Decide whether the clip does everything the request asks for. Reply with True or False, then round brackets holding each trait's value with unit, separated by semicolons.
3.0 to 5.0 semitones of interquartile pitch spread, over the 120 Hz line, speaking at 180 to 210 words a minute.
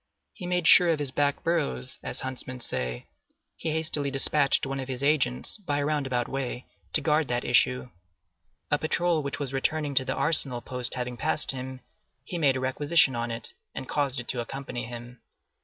True (3.3 semitones; 135 Hz; 190 wpm)